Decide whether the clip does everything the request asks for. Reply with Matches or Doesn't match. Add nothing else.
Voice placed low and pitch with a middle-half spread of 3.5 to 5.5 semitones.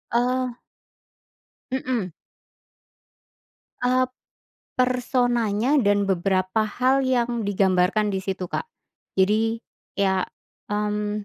Doesn't match